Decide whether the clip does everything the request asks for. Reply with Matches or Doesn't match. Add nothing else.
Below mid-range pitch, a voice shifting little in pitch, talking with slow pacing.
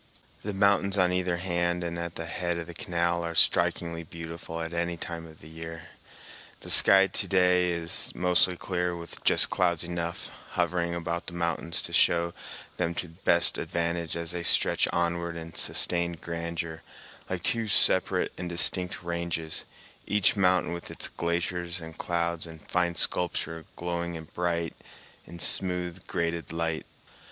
Doesn't match